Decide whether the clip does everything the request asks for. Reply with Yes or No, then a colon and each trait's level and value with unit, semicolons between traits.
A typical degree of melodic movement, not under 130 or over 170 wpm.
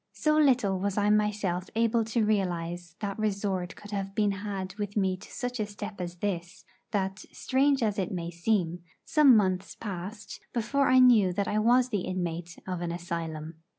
No: average, 3.3 semitones; average, 185 wpm